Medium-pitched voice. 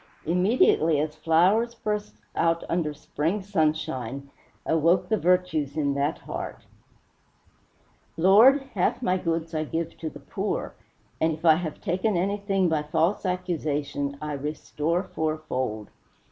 Yes: medium, 165 Hz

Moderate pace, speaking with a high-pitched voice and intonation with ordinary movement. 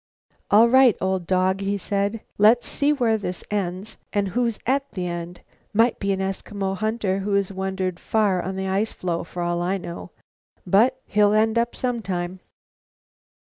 Yes: average, 170 wpm; high, 195 Hz; average, 3.1 semitones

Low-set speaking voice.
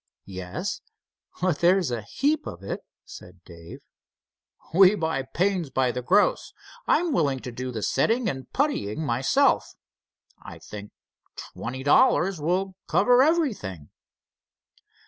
No: medium, 150 Hz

